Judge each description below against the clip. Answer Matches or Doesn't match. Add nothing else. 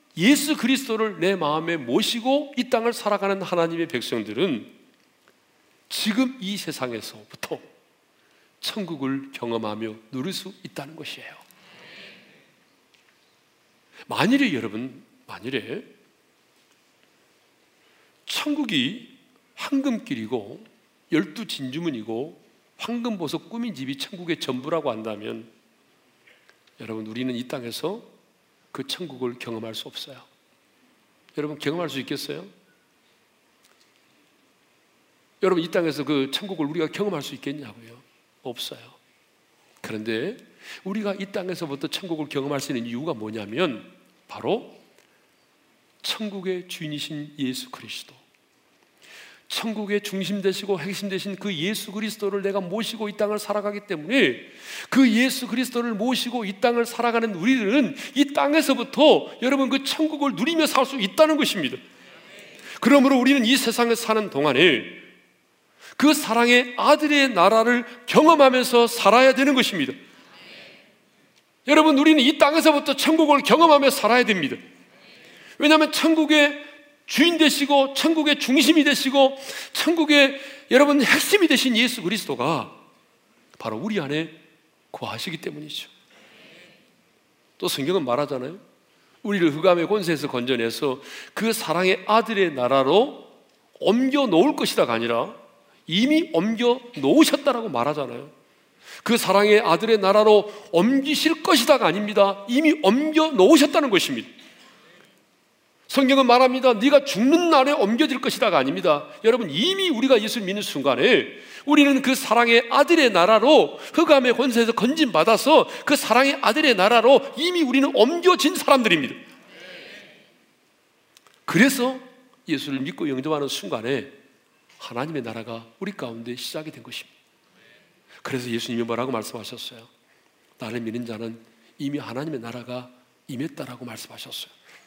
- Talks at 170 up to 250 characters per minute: Doesn't match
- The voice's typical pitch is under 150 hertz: Doesn't match